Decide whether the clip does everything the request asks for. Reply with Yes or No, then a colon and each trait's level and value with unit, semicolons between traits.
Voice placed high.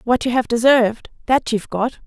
Yes: high, 240 Hz